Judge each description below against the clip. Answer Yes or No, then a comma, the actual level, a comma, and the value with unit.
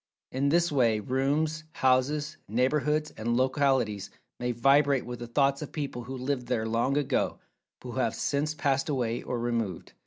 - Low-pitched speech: Yes, low, 130 Hz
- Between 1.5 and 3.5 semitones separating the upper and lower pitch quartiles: Yes, average, 3.2 semitones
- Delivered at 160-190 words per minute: Yes, average, 165 wpm